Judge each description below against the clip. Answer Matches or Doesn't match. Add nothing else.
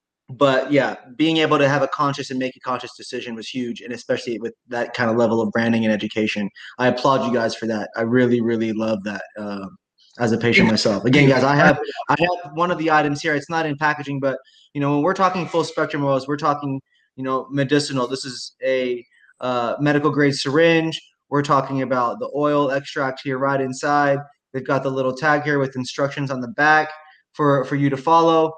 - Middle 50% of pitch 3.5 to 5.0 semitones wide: Doesn't match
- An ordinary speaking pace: Doesn't match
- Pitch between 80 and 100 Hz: Doesn't match